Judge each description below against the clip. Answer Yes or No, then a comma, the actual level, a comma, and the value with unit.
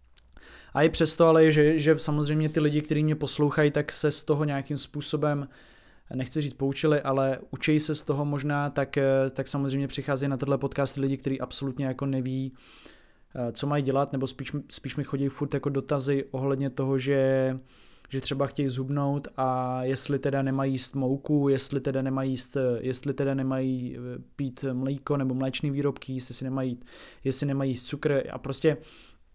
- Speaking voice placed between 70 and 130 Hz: No, medium, 140 Hz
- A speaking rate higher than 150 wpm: Yes, fast, 170 wpm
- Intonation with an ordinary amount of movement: No, narrow, 1.6 semitones